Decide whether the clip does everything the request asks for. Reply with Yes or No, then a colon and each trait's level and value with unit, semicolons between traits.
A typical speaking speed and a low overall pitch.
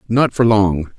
Yes: average, 185 wpm; low, 105 Hz